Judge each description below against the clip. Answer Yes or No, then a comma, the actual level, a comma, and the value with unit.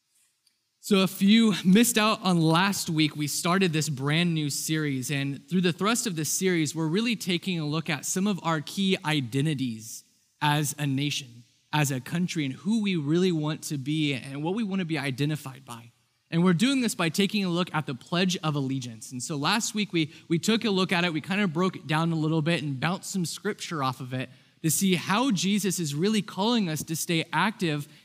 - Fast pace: Yes, fast, 220 wpm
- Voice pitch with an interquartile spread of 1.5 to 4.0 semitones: No, average, 4.5 semitones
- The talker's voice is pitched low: No, medium, 165 Hz